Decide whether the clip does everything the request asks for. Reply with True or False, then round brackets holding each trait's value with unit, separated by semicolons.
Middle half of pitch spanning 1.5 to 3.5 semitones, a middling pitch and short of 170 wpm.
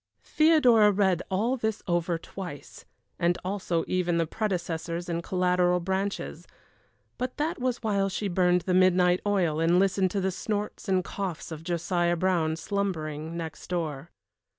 True (2.8 semitones; 180 Hz; 150 wpm)